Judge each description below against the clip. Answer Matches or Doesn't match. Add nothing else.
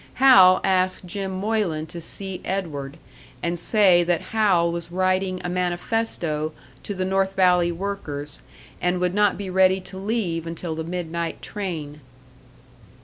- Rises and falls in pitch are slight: Matches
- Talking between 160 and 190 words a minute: Doesn't match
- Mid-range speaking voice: Matches